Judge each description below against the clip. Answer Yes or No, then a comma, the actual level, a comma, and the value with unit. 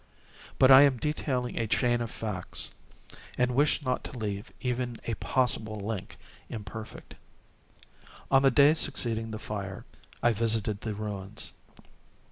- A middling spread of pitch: Yes, average, 3.0 semitones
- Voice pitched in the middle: No, low, 115 Hz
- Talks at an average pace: No, slow, 130 wpm